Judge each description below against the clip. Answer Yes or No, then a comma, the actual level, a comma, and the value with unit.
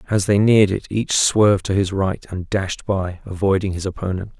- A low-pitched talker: Yes, low, 100 Hz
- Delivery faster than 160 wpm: Yes, fast, 205 wpm